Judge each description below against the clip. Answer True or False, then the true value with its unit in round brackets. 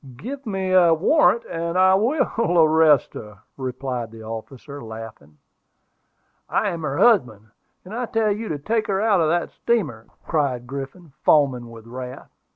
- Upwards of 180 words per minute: False (160 wpm)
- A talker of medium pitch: True (155 Hz)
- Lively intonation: True (7.9 semitones)